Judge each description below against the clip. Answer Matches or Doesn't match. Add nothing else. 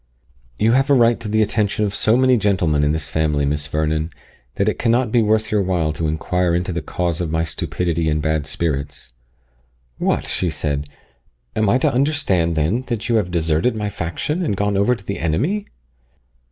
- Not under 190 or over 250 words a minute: Matches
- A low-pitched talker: Matches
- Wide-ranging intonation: Matches